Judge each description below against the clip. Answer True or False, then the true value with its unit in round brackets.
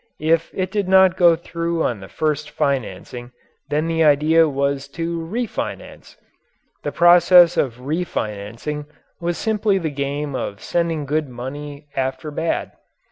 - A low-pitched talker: False (155 Hz)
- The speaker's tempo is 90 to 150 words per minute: True (135 wpm)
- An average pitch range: True (3.5 semitones)